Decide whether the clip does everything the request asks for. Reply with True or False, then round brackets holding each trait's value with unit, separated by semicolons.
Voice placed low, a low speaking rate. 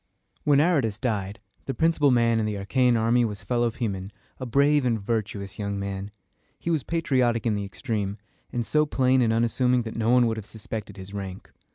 False (115 Hz; 200 wpm)